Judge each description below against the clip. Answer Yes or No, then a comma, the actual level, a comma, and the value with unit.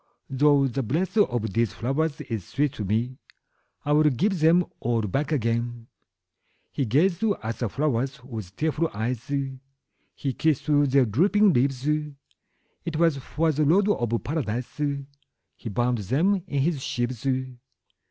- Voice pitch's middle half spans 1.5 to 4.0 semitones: No, average, 4.9 semitones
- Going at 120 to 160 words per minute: Yes, average, 140 wpm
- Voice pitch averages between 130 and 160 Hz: Yes, low, 135 Hz